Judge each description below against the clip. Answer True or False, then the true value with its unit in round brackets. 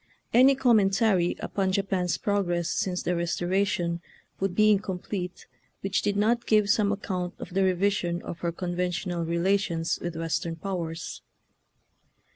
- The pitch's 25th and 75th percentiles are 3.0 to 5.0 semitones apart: False (2.6 semitones)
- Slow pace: False (145 wpm)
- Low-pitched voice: False (185 Hz)